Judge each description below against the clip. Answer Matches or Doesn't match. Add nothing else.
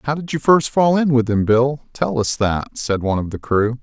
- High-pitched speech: Doesn't match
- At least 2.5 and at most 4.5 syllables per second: Doesn't match